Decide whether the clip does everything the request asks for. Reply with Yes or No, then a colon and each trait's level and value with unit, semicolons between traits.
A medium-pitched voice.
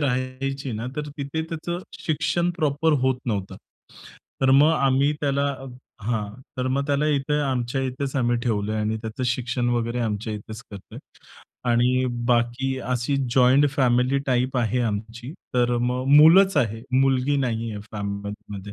No: low, 125 Hz